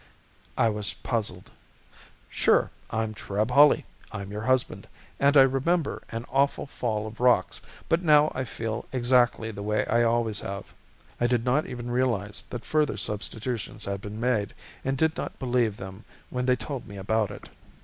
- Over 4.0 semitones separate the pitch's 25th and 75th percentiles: No, average, 3.5 semitones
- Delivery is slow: No, average, 170 wpm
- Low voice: Yes, low, 120 Hz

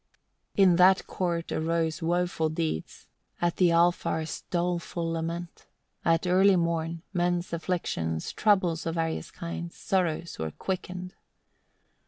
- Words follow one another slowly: Yes, slow, 120 wpm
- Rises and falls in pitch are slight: Yes, narrow, 1.5 semitones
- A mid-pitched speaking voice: Yes, medium, 170 Hz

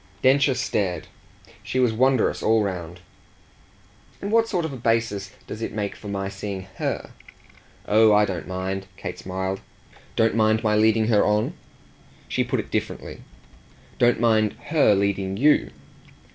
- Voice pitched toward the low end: Yes, low, 110 Hz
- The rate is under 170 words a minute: Yes, average, 150 wpm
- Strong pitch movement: No, average, 3.4 semitones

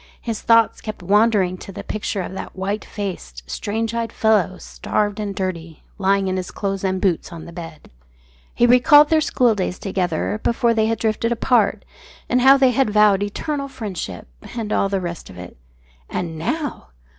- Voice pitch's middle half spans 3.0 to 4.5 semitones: Yes, average, 3.8 semitones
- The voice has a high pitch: Yes, high, 205 Hz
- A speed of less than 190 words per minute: Yes, average, 180 wpm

